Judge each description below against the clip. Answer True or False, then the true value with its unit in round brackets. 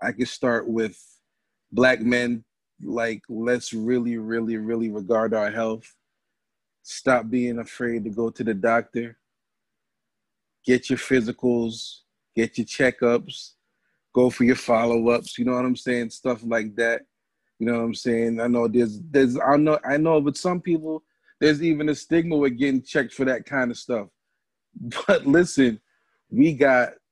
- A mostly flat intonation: True (2.2 semitones)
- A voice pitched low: True (120 Hz)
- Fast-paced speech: False (160 wpm)